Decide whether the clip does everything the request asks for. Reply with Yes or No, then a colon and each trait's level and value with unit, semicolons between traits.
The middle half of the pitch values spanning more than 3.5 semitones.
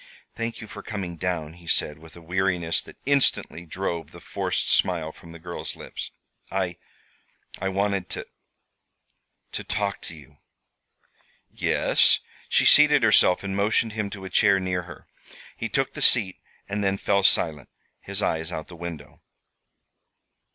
No: average, 3.2 semitones